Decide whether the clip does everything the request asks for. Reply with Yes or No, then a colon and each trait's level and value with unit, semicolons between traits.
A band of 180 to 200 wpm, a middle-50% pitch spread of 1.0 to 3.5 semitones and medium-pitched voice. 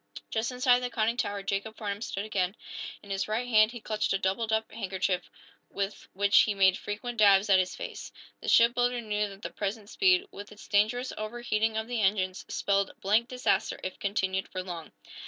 No: average, 190 wpm; average, 2.8 semitones; high, 210 Hz